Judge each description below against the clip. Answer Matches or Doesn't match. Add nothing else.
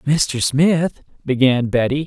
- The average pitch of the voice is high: Doesn't match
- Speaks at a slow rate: Matches